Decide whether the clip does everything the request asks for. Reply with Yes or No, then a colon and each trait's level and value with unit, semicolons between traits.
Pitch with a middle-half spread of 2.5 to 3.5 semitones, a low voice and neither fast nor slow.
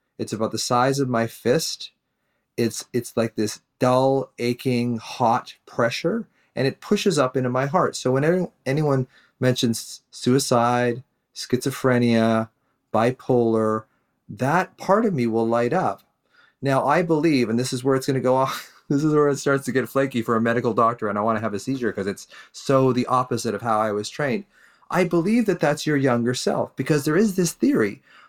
Yes: average, 3.0 semitones; low, 125 Hz; average, 190 wpm